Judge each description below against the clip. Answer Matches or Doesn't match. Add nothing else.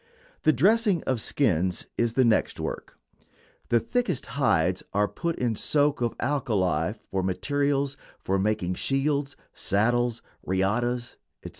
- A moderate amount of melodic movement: Doesn't match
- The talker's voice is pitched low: Matches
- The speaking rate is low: Matches